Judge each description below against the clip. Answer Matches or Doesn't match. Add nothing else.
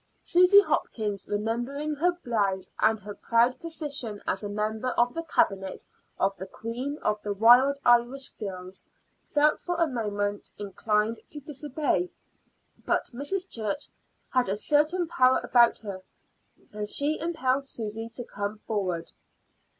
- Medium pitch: Doesn't match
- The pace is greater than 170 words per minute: Doesn't match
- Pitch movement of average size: Doesn't match